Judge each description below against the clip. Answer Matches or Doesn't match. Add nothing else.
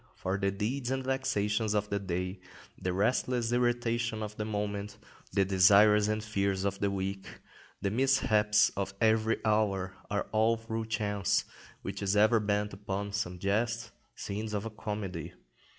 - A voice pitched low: Matches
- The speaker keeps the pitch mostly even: Matches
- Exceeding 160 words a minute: Doesn't match